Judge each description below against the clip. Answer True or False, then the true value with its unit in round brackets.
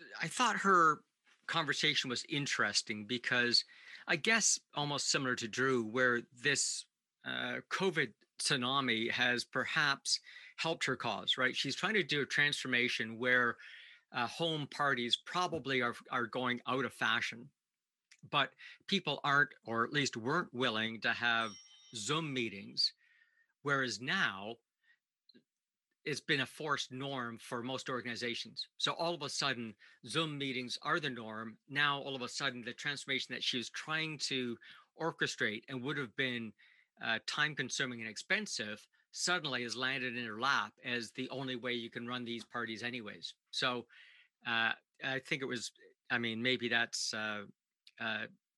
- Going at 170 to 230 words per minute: False (150 wpm)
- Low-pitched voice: True (125 Hz)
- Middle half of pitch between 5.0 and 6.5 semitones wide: False (3.5 semitones)